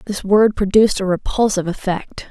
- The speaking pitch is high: Yes, high, 200 Hz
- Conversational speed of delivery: Yes, average, 155 wpm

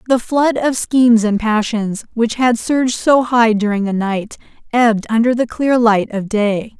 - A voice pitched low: No, high, 230 Hz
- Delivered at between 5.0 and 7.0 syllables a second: No, 4.4 syllables/s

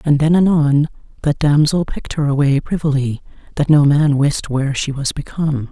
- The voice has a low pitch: No, medium, 145 Hz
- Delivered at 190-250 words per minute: No, average, 180 wpm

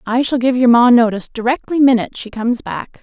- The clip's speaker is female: Yes, female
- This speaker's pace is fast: Yes, fast, 220 wpm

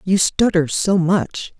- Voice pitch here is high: No, medium, 180 Hz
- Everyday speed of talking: Yes, average, 150 wpm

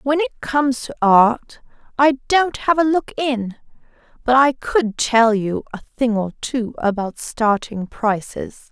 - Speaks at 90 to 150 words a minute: No, average, 160 wpm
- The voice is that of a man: No, female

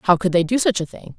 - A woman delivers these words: Yes, female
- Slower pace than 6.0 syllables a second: No, 6.1 syllables/s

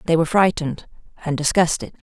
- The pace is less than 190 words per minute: Yes, average, 140 wpm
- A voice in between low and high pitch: Yes, medium, 165 Hz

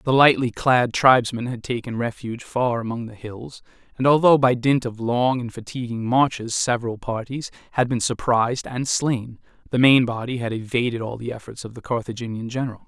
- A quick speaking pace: No, average, 180 wpm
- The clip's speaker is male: Yes, male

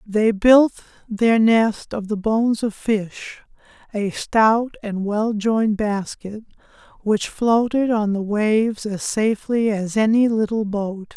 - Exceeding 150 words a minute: No, average, 140 wpm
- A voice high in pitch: Yes, high, 215 Hz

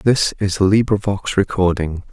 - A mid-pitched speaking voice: No, low, 100 Hz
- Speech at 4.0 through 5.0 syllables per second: Yes, 4.6 syllables/s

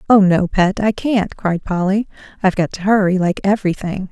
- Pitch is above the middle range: Yes, high, 195 Hz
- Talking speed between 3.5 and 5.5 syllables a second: Yes, 5.4 syllables/s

